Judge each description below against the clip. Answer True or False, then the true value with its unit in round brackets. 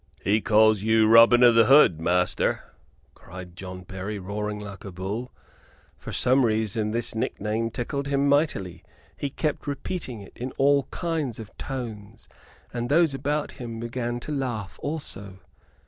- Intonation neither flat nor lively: True (4.8 semitones)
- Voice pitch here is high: False (115 Hz)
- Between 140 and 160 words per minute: True (155 wpm)